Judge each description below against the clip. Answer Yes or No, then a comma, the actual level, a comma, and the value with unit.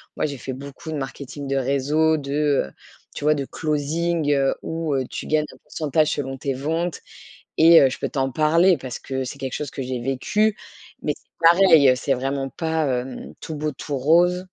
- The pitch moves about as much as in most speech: Yes, average, 3.0 semitones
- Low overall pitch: No, medium, 145 Hz